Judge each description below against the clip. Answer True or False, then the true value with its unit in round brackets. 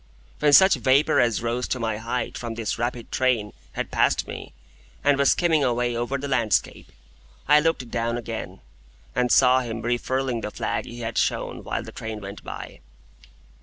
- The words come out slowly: False (175 wpm)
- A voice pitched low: True (120 Hz)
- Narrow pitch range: True (2.2 semitones)